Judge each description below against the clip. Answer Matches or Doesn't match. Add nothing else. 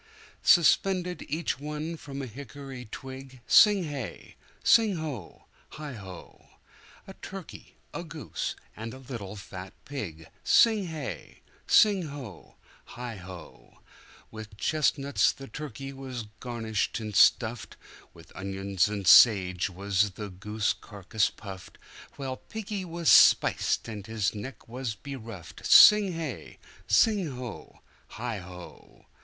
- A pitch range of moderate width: Doesn't match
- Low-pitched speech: Matches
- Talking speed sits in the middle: Doesn't match